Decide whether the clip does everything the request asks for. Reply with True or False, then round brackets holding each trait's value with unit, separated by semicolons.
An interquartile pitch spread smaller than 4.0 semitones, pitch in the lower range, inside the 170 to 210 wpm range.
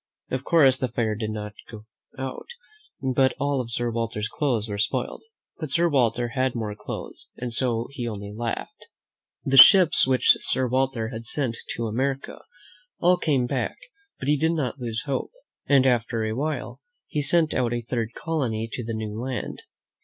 True (3.2 semitones; 125 Hz; 175 wpm)